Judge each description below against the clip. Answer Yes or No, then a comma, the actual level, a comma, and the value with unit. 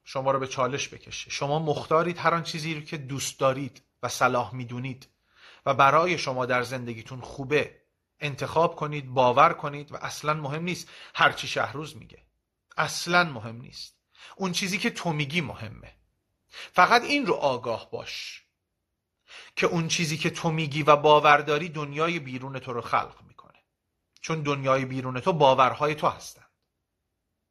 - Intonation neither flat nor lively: Yes, average, 3.9 semitones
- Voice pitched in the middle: Yes, medium, 145 Hz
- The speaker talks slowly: No, average, 150 wpm